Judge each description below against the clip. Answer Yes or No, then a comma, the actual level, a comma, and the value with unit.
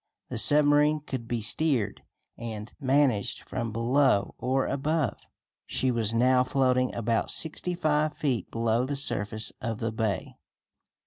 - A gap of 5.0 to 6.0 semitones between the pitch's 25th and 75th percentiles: No, average, 4.1 semitones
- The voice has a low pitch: Yes, low, 125 Hz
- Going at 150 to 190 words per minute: No, slow, 135 wpm